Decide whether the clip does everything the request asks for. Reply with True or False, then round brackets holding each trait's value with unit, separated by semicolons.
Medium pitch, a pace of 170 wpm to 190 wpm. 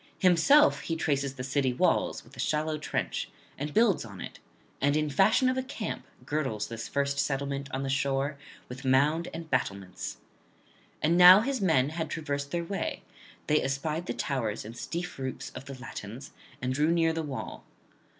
True (145 Hz; 180 wpm)